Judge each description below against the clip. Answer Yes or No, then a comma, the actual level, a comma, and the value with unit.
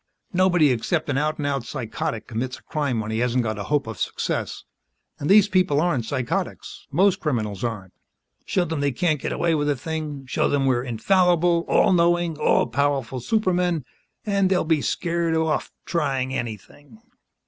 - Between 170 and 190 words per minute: Yes, average, 175 wpm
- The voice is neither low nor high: Yes, medium, 145 Hz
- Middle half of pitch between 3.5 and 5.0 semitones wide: No, wide, 5.5 semitones